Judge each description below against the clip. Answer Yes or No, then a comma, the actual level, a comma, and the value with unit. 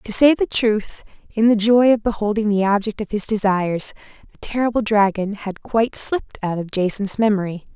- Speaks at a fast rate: No, average, 185 wpm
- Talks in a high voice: Yes, high, 210 Hz